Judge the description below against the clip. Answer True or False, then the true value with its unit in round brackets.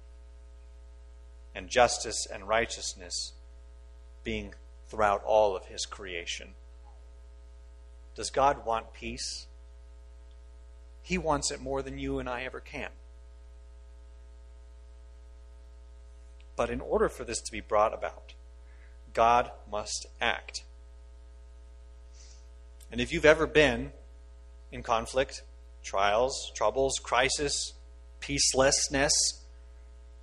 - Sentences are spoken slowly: True (95 wpm)